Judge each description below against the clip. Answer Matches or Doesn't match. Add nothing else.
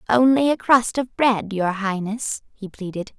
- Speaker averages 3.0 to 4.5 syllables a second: Matches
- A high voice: Matches